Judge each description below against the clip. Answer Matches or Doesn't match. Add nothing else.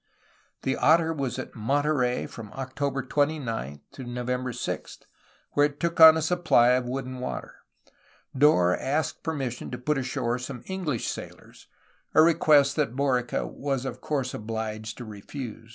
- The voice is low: Matches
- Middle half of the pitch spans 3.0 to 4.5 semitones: Matches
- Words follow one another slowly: Doesn't match